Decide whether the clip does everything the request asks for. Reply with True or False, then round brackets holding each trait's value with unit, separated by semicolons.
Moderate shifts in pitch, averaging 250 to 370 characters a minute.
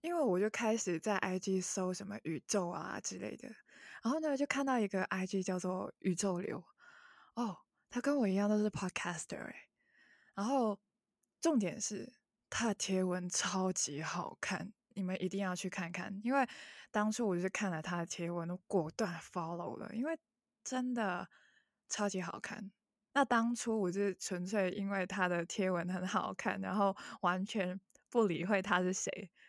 True (3.3 semitones; 265 characters per minute)